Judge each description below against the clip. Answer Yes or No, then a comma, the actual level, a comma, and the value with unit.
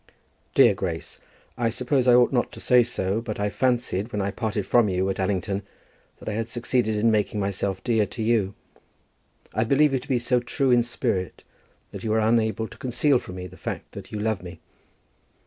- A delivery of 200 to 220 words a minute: Yes, fast, 205 wpm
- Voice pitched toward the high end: No, low, 110 Hz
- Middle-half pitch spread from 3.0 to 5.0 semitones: Yes, average, 3.3 semitones